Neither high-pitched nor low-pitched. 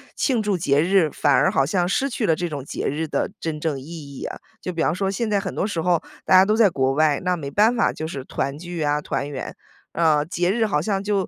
Yes: medium, 170 Hz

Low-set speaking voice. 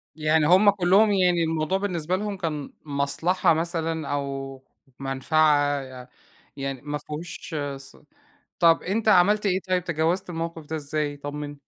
No: medium, 160 Hz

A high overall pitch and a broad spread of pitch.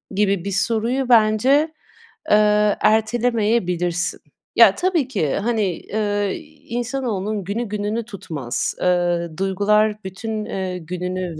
No: high, 210 Hz; average, 3.7 semitones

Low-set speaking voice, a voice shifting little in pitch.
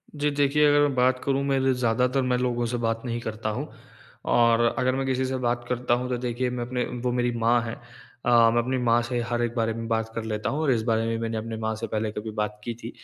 Yes: low, 120 Hz; narrow, 2.0 semitones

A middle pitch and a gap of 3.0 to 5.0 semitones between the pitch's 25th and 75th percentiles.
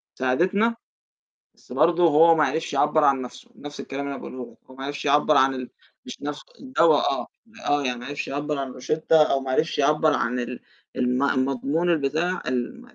Yes: medium, 145 Hz; average, 3.4 semitones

